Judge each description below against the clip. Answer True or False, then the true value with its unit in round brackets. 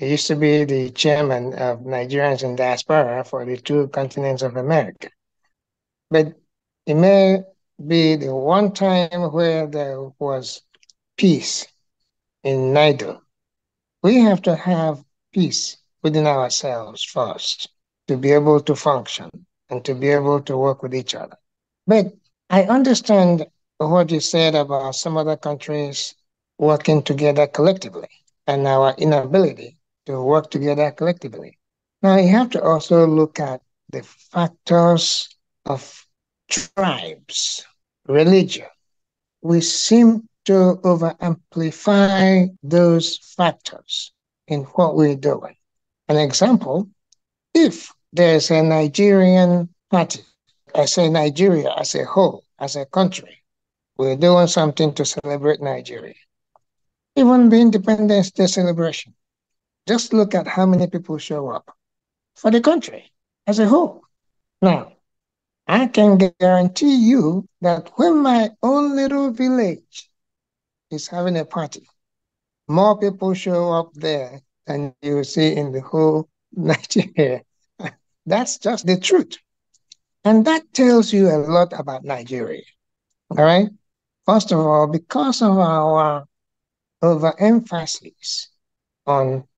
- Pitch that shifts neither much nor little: True (4.6 semitones)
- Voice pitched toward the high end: False (165 Hz)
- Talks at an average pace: False (125 wpm)